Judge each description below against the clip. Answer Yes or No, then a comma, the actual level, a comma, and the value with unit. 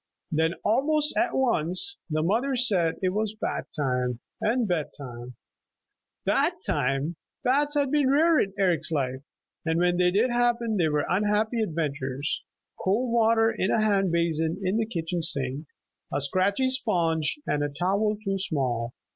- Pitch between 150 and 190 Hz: Yes, medium, 185 Hz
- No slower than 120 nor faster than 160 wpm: Yes, average, 155 wpm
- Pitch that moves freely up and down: Yes, wide, 6.8 semitones